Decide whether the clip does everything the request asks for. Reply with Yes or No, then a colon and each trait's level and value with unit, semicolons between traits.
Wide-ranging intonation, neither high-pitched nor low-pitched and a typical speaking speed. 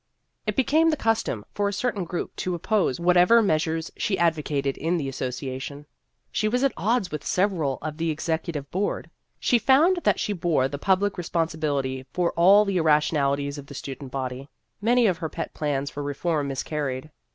Yes: wide, 5.7 semitones; medium, 160 Hz; average, 185 wpm